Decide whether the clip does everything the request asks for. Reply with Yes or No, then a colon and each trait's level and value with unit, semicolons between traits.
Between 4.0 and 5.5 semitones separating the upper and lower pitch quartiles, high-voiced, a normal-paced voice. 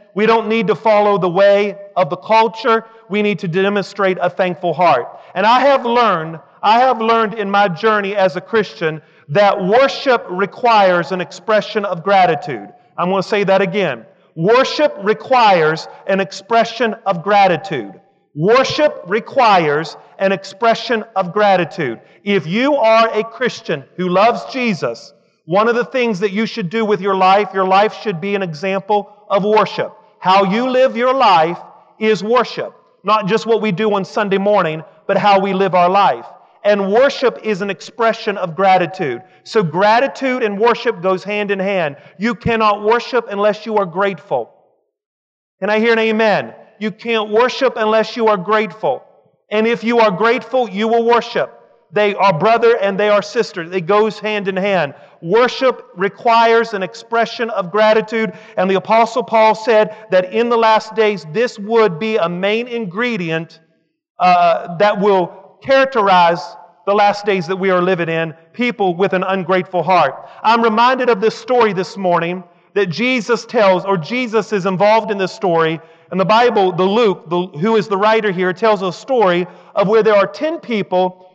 No: average, 3.2 semitones; high, 210 Hz; average, 170 wpm